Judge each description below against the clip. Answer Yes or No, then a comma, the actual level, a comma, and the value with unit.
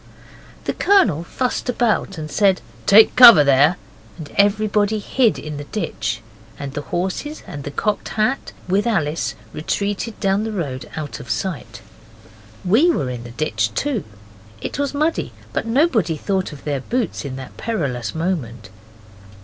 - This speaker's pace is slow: No, average, 155 wpm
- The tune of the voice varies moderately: No, wide, 7.3 semitones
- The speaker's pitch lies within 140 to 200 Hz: Yes, medium, 185 Hz